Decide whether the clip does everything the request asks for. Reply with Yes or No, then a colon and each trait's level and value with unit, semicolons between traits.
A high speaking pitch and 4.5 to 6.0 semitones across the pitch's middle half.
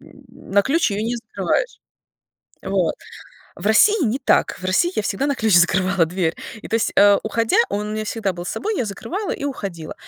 Yes: high, 215 Hz; average, 5.0 semitones